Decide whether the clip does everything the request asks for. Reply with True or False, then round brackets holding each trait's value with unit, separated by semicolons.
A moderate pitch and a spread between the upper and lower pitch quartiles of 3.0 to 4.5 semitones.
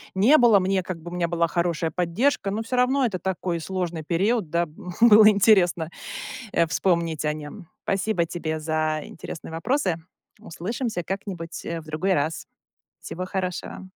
True (180 Hz; 3.4 semitones)